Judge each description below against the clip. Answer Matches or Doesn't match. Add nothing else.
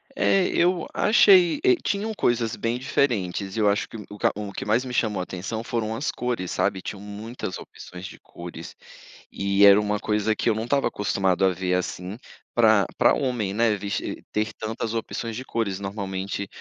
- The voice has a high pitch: Doesn't match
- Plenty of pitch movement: Doesn't match